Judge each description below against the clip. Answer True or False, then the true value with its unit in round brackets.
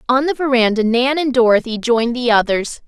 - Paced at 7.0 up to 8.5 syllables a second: False (5.6 syllables/s)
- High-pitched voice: True (245 Hz)